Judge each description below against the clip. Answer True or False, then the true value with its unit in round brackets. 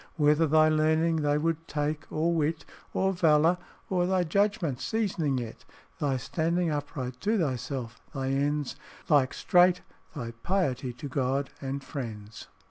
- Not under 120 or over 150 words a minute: True (140 wpm)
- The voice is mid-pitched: True (150 Hz)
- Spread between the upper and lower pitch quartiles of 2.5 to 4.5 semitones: True (3.8 semitones)